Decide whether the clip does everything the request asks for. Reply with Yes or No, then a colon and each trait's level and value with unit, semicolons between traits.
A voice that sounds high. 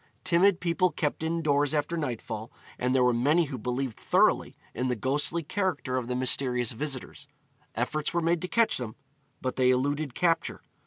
No: medium, 140 Hz